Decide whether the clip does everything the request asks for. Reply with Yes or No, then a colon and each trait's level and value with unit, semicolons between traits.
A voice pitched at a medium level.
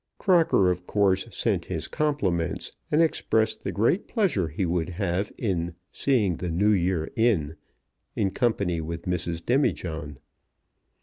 No: very low, 95 Hz